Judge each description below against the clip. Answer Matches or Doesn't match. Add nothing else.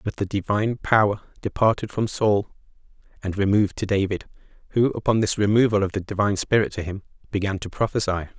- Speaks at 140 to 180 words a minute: Matches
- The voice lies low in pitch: Matches